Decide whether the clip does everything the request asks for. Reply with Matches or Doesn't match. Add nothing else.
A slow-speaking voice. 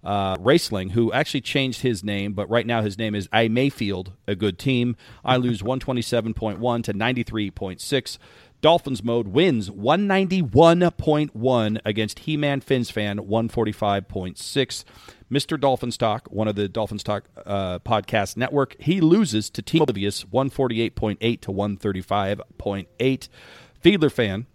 Matches